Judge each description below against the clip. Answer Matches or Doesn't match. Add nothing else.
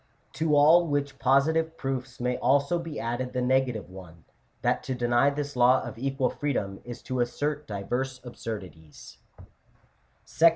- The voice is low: Matches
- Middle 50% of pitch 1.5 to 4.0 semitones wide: Matches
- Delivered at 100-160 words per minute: Matches